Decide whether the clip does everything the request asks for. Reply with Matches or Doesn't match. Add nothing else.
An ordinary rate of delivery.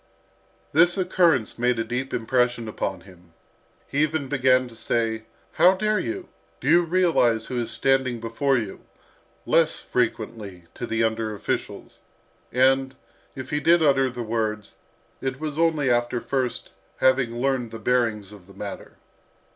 Matches